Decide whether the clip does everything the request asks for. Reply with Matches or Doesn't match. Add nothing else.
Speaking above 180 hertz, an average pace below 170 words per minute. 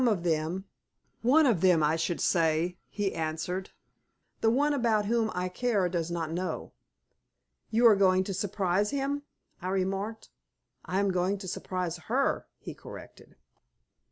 Matches